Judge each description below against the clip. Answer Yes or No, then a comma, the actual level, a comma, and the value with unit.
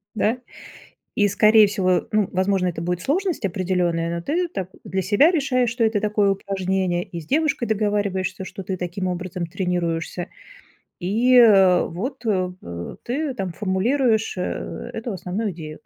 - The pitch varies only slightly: No, average, 3.8 semitones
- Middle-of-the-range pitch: No, high, 195 Hz